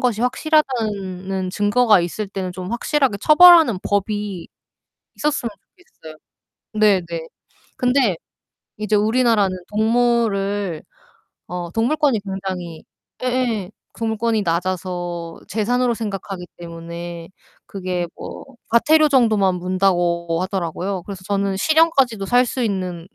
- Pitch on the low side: No, high, 200 Hz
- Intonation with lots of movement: No, average, 4.6 semitones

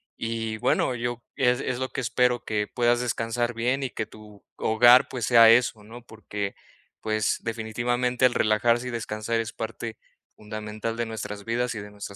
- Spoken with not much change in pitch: Yes, narrow, 2.0 semitones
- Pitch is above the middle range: No, low, 115 Hz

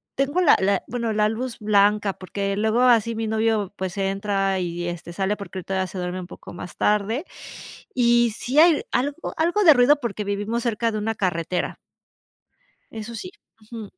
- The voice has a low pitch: No, high, 215 Hz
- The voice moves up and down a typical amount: Yes, average, 3.4 semitones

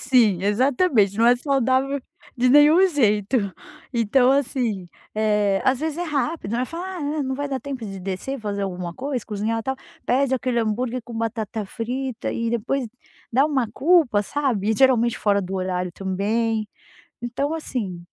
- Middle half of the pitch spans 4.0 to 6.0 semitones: Yes, average, 4.6 semitones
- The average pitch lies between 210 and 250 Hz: Yes, high, 240 Hz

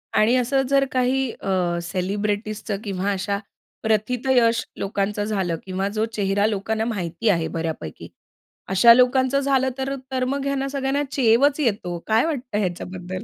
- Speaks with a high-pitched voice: Yes, high, 220 Hz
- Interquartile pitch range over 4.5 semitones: Yes, average, 5.2 semitones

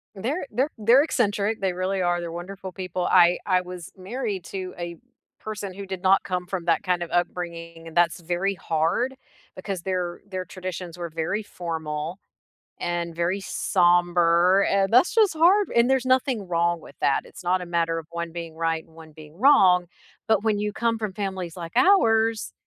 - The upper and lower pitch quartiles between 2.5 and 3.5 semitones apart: Yes, average, 3.2 semitones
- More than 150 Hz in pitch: Yes, medium, 185 Hz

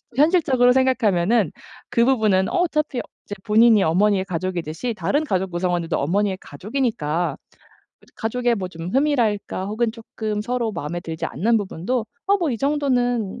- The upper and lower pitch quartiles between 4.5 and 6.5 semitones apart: Yes, average, 5.2 semitones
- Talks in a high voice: Yes, high, 215 Hz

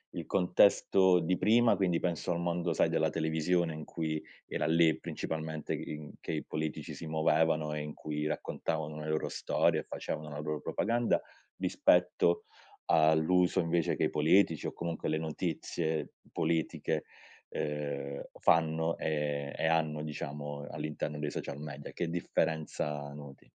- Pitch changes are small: Yes, narrow, 1.9 semitones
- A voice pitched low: Yes, very low, 80 Hz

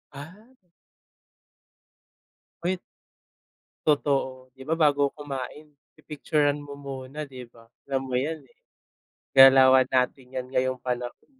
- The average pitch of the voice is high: No, low, 135 Hz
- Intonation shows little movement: Yes, narrow, 2.3 semitones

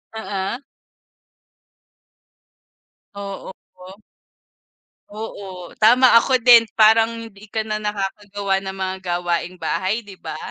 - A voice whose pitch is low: No, high, 200 Hz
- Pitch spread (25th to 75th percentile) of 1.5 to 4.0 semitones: Yes, narrow, 2.6 semitones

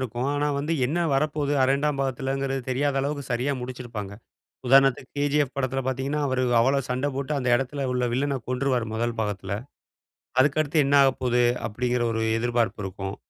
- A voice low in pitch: Yes, low, 130 Hz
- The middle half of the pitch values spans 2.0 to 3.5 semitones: Yes, narrow, 2.4 semitones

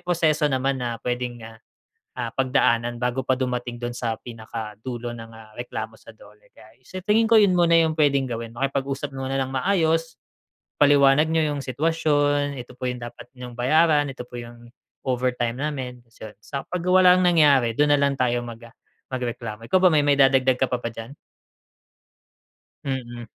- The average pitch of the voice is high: No, low, 130 Hz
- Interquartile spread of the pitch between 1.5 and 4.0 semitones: Yes, average, 3.5 semitones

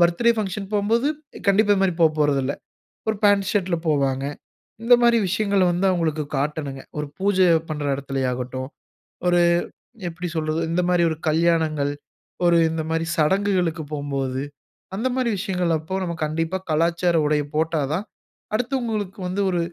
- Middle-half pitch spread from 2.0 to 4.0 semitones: No, average, 4.4 semitones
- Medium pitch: Yes, medium, 170 Hz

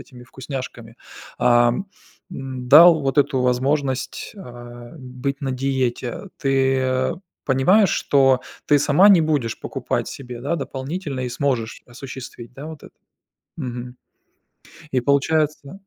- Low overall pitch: Yes, low, 130 Hz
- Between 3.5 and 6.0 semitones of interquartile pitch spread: No, narrow, 2.5 semitones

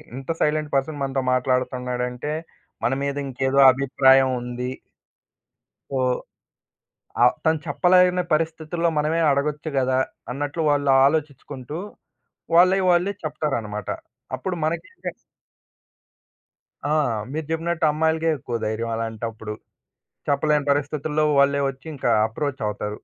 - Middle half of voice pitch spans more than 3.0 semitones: Yes, average, 3.6 semitones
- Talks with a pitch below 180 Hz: Yes, medium, 140 Hz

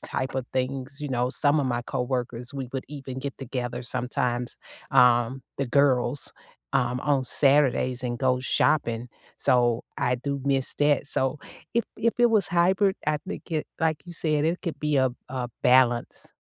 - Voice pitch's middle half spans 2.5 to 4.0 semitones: Yes, average, 2.9 semitones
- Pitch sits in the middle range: No, low, 130 Hz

